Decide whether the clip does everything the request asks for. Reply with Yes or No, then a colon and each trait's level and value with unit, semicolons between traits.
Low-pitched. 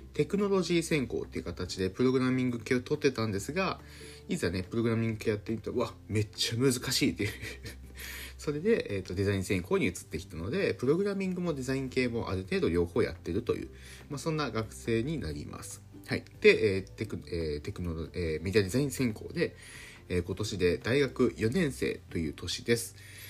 Yes: low, 110 Hz